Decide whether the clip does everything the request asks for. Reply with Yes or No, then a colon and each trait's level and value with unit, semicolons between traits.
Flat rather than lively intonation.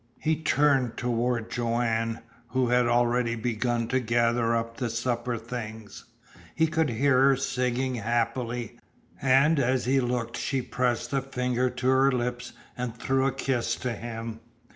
Yes: narrow, 1.9 semitones